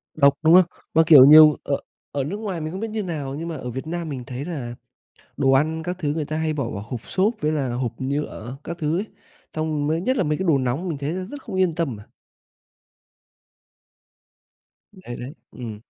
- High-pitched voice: No, medium, 155 Hz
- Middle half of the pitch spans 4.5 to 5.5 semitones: No, average, 4.0 semitones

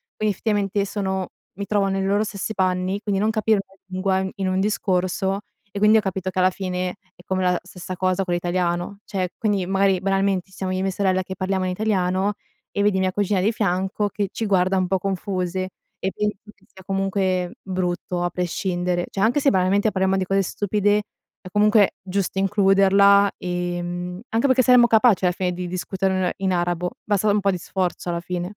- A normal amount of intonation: No, narrow, 1.7 semitones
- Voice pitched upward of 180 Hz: Yes, high, 190 Hz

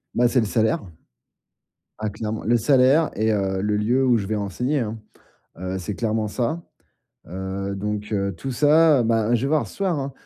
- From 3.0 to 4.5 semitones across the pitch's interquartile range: Yes, average, 4.1 semitones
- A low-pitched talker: Yes, low, 110 Hz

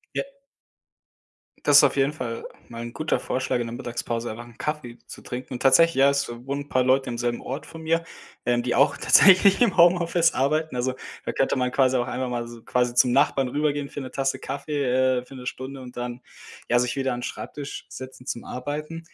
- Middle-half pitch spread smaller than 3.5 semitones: Yes, average, 2.9 semitones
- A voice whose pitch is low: Yes, low, 130 Hz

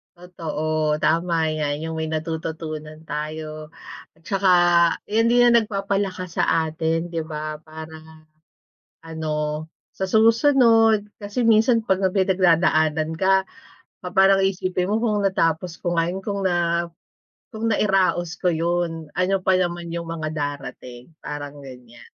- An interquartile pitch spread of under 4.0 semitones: Yes, average, 3.5 semitones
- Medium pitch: Yes, medium, 170 Hz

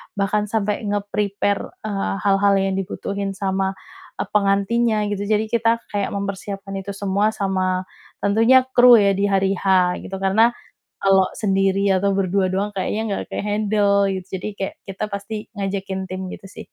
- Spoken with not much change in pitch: Yes, narrow, 1.3 semitones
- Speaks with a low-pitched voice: No, high, 200 Hz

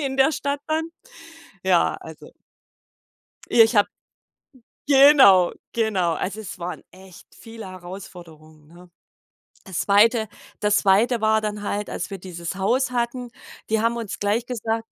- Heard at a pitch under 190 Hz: No, high, 210 Hz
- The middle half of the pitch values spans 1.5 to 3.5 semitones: No, average, 4.2 semitones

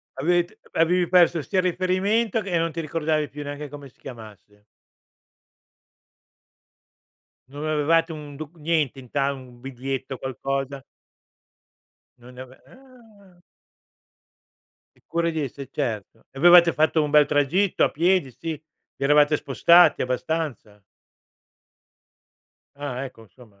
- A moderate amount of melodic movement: Yes, average, 4.1 semitones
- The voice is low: No, medium, 150 Hz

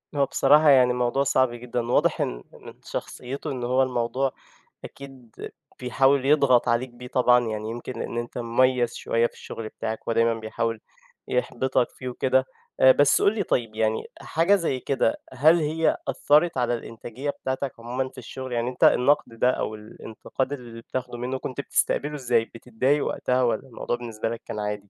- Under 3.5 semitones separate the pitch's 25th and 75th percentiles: Yes, narrow, 2.4 semitones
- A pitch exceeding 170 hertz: No, low, 125 Hz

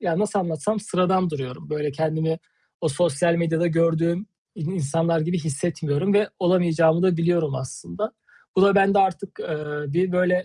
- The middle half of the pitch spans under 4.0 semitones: Yes, average, 2.7 semitones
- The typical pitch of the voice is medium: Yes, medium, 170 Hz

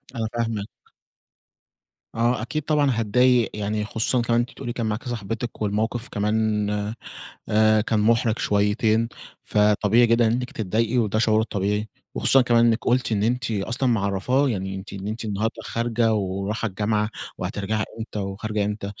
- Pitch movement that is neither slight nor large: No, narrow, 2.2 semitones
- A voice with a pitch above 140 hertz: No, low, 110 Hz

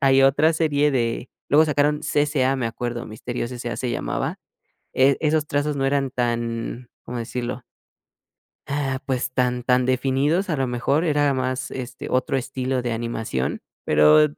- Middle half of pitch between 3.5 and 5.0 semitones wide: No, average, 2.8 semitones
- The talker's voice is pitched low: Yes, low, 130 Hz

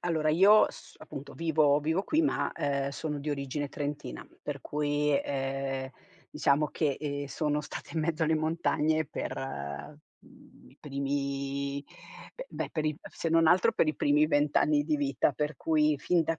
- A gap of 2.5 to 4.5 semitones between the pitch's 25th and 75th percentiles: No, narrow, 2.1 semitones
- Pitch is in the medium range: Yes, medium, 150 Hz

